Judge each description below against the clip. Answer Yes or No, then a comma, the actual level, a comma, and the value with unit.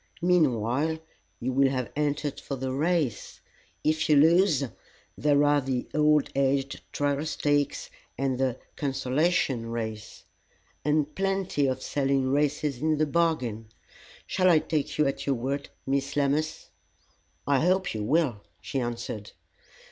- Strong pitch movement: No, average, 2.8 semitones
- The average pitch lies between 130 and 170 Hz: Yes, medium, 140 Hz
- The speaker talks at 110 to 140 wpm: Yes, slow, 135 wpm